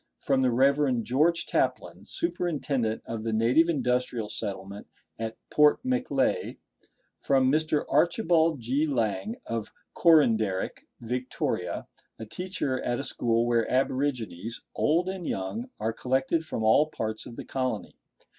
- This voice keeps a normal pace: No, slow, 130 wpm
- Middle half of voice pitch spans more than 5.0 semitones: Yes, wide, 5.5 semitones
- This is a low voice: Yes, low, 130 Hz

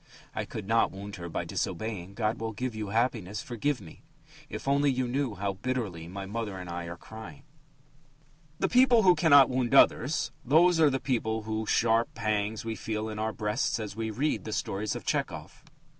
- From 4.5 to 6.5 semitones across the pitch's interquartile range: No, average, 4.0 semitones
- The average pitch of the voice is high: No, low, 110 Hz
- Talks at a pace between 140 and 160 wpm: No, average, 190 wpm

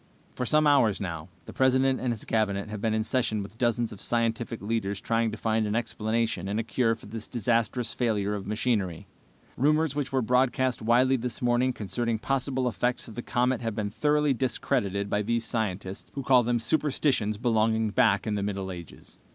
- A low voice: Yes, low, 115 Hz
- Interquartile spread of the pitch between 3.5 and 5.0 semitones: No, average, 3.1 semitones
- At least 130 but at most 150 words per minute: No, average, 190 wpm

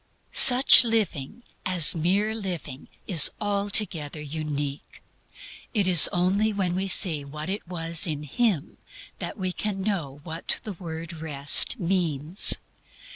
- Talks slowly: Yes, slow, 130 wpm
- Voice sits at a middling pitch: Yes, medium, 175 Hz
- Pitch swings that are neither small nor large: Yes, average, 4.6 semitones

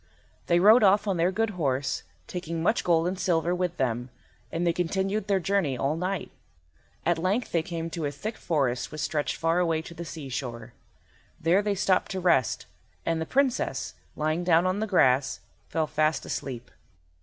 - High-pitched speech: No, medium, 170 Hz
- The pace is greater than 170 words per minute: Yes, average, 180 wpm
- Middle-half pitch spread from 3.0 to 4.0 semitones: Yes, average, 3.4 semitones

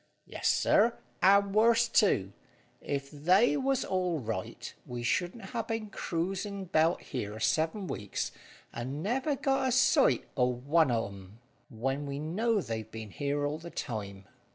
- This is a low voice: No, medium, 160 Hz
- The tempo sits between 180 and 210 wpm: No, average, 155 wpm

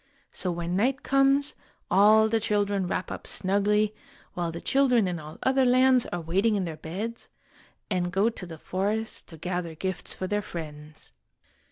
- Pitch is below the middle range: No, high, 195 Hz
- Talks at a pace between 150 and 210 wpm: Yes, average, 170 wpm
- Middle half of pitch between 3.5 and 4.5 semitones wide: Yes, average, 4.2 semitones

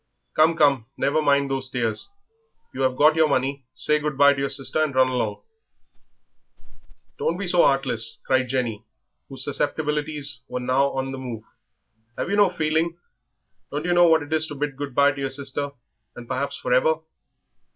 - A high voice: No, medium, 140 Hz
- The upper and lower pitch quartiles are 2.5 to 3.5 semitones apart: Yes, average, 2.8 semitones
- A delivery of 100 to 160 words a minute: No, average, 185 wpm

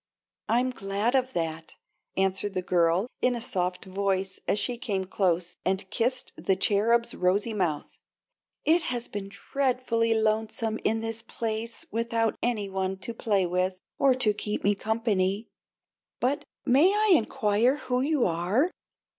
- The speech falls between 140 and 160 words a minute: Yes, average, 145 wpm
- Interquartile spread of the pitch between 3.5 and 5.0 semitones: Yes, average, 4.1 semitones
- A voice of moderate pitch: No, high, 215 Hz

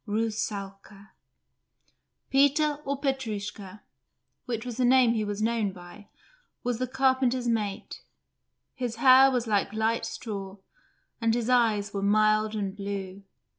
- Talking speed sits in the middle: No, slow, 130 wpm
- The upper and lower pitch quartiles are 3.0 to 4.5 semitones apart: Yes, average, 3.5 semitones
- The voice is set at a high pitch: Yes, high, 220 Hz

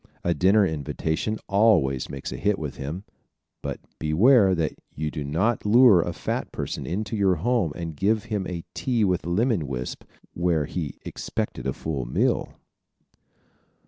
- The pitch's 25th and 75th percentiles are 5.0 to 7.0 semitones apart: Yes, wide, 5.5 semitones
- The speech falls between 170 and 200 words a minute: No, average, 155 wpm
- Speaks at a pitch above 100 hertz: No, very low, 90 Hz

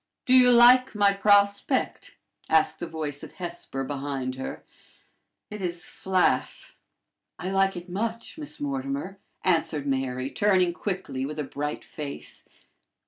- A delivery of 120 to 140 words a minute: Yes, slow, 135 wpm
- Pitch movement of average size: No, wide, 6.2 semitones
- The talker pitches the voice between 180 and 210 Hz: Yes, medium, 185 Hz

